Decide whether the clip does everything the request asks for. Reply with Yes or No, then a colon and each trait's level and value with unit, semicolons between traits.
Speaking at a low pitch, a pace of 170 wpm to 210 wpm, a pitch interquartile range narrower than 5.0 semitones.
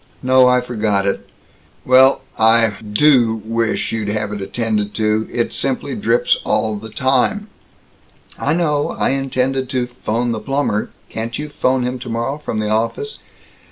No: low, 120 Hz; average, 155 wpm; average, 3.3 semitones